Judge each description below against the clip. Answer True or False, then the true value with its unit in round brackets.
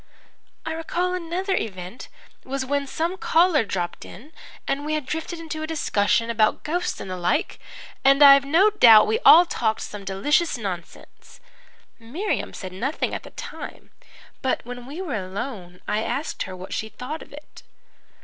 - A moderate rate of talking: True (170 wpm)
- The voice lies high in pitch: True (275 Hz)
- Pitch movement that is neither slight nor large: False (7.3 semitones)